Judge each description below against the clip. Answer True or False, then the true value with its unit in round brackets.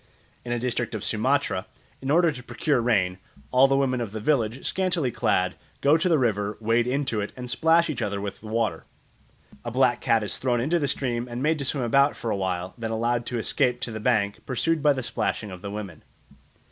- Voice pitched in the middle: False (120 Hz)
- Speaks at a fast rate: True (225 wpm)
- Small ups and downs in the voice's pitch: False (4.2 semitones)